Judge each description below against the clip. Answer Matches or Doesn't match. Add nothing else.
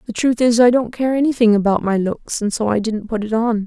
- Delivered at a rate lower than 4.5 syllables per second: Doesn't match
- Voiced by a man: Doesn't match